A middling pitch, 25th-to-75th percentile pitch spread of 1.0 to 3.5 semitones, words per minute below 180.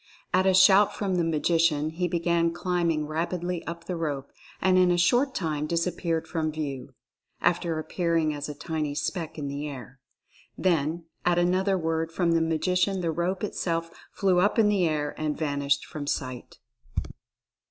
Yes: medium, 165 Hz; average, 2.8 semitones; average, 170 wpm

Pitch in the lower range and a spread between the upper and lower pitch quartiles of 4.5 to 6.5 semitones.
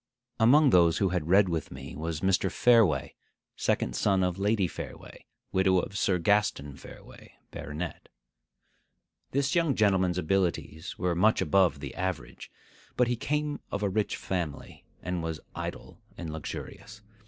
No: very low, 95 Hz; average, 3.9 semitones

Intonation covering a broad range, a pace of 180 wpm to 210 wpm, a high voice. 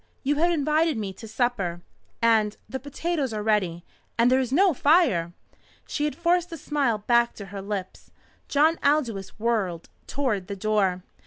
No: wide, 6.7 semitones; average, 165 wpm; high, 235 Hz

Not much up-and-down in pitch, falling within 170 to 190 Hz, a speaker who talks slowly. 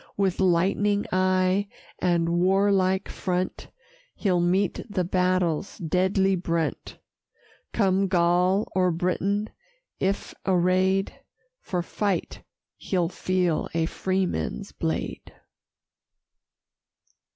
Yes: narrow, 1.6 semitones; medium, 185 Hz; slow, 85 wpm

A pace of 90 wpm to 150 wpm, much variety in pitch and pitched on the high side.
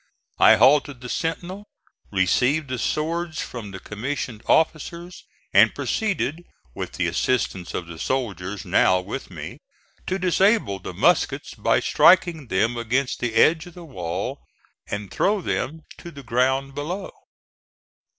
No: average, 140 wpm; wide, 7.4 semitones; low, 135 Hz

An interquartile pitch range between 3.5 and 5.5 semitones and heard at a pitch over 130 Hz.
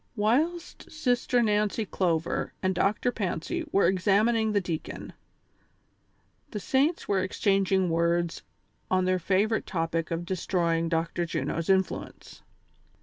Yes: average, 4.0 semitones; high, 190 Hz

